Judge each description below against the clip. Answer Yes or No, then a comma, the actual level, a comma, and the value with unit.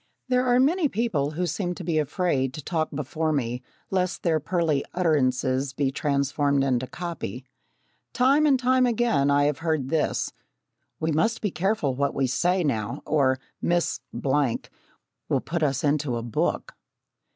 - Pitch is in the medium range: Yes, medium, 155 Hz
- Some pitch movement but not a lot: Yes, average, 4.8 semitones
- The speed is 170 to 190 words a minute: No, average, 160 wpm